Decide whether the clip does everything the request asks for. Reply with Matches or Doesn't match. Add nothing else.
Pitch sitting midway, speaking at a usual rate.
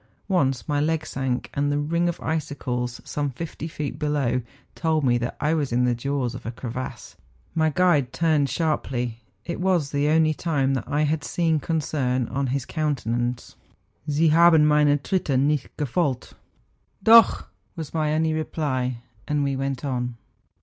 Matches